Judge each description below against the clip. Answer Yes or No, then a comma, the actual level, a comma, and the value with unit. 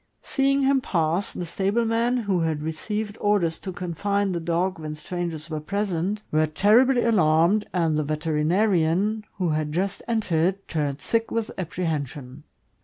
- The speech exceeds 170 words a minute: No, average, 150 wpm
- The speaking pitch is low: No, medium, 180 Hz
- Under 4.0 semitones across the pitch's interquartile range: No, average, 4.8 semitones